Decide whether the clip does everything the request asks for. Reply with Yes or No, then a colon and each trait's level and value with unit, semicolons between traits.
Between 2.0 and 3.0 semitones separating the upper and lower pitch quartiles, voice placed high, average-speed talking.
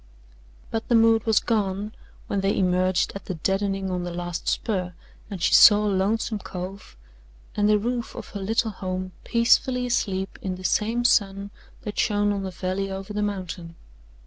Yes: narrow, 2.5 semitones; high, 200 Hz; average, 170 wpm